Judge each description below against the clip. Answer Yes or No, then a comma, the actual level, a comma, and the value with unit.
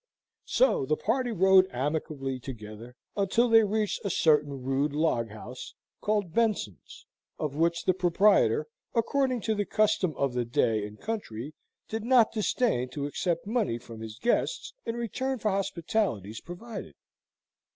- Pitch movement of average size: No, wide, 9.0 semitones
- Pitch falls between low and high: Yes, medium, 175 Hz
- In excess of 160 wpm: No, average, 145 wpm